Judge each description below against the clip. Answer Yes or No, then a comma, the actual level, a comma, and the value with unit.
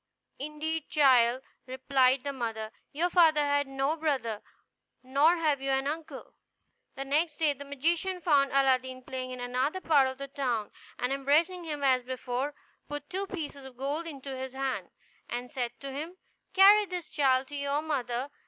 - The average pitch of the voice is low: No, very high, 275 Hz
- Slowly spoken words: No, average, 170 wpm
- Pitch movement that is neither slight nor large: Yes, average, 3.0 semitones